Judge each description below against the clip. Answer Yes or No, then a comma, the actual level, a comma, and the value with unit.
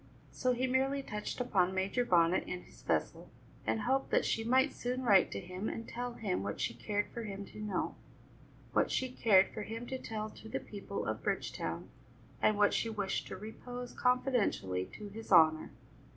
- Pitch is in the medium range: No, high, 215 Hz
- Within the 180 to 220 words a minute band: Yes, average, 190 wpm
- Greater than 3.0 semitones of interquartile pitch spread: Yes, average, 4.3 semitones